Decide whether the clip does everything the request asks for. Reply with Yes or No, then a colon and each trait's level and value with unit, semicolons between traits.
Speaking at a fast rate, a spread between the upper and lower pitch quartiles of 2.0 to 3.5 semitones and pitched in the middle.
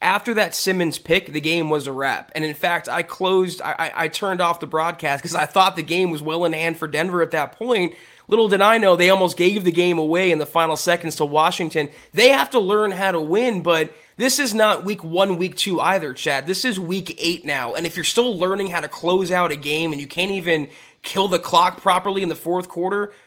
Yes: fast, 245 wpm; average, 3.0 semitones; medium, 175 Hz